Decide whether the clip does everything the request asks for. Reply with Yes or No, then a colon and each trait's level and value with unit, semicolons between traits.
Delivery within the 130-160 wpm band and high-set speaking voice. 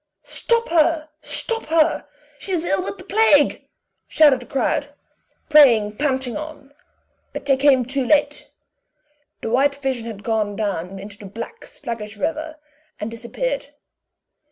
Yes: average, 140 wpm; very high, 275 Hz